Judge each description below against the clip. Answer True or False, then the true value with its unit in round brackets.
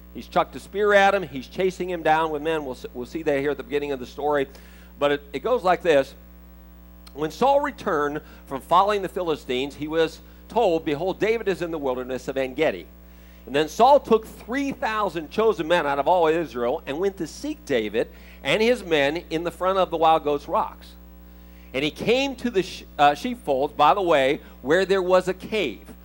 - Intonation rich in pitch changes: True (6.5 semitones)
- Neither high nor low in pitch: True (155 Hz)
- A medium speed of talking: False (210 wpm)